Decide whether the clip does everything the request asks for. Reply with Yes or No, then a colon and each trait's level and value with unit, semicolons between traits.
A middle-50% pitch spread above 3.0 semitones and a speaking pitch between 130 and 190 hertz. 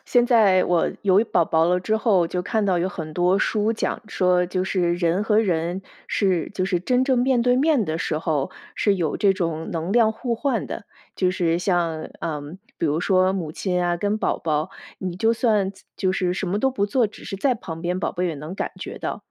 Yes: average, 3.8 semitones; medium, 185 Hz